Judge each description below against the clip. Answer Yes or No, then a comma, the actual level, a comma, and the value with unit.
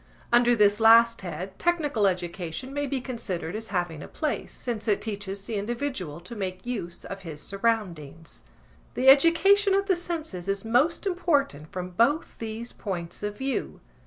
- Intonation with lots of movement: Yes, wide, 6.5 semitones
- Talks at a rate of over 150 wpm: Yes, average, 160 wpm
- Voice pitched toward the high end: Yes, high, 220 Hz